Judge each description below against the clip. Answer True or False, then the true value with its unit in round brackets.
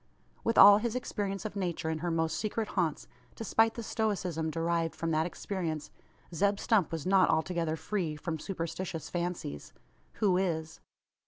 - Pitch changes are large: False (3.9 semitones)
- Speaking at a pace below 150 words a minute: False (155 wpm)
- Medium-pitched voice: True (175 Hz)